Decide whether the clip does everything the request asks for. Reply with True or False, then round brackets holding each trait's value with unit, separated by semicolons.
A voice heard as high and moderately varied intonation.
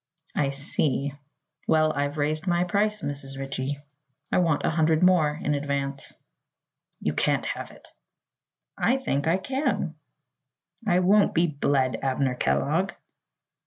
False (150 Hz; 4.1 semitones)